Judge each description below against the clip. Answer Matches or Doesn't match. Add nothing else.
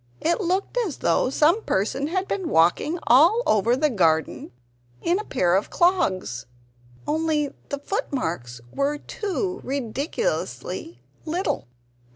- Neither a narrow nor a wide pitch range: Doesn't match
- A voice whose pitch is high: Matches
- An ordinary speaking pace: Doesn't match